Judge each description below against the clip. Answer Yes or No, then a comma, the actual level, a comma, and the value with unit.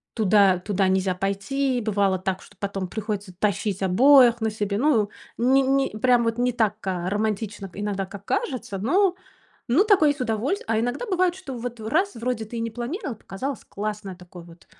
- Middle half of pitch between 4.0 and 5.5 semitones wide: Yes, average, 4.3 semitones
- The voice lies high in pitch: Yes, high, 220 Hz